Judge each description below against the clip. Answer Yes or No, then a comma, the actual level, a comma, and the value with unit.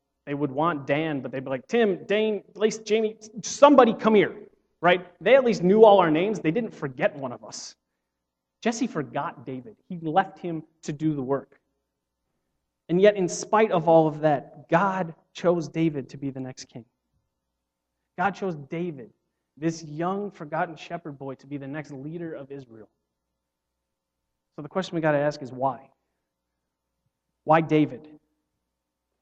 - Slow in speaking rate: No, average, 165 wpm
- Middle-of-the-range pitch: Yes, medium, 150 Hz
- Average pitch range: No, wide, 6.5 semitones